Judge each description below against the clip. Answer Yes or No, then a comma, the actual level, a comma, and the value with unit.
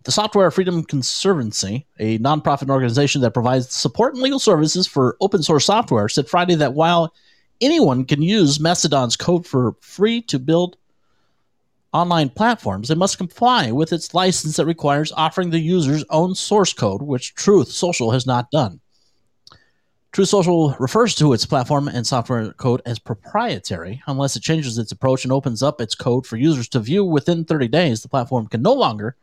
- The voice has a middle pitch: Yes, medium, 150 Hz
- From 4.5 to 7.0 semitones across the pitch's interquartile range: Yes, wide, 5.4 semitones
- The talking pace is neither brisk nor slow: Yes, average, 175 wpm